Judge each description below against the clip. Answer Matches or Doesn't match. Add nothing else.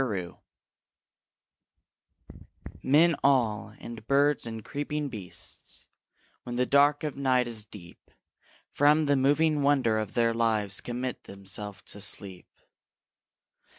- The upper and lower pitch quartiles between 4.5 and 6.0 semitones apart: Matches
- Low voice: Matches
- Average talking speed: Doesn't match